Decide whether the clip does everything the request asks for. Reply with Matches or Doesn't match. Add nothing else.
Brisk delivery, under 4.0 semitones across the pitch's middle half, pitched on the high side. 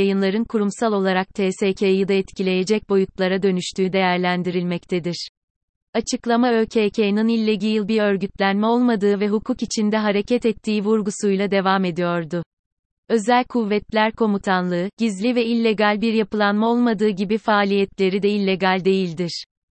Doesn't match